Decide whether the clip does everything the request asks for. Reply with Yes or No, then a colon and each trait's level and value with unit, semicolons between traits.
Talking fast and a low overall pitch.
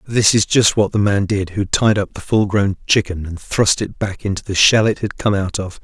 Yes: fast, 270 wpm; low, 100 Hz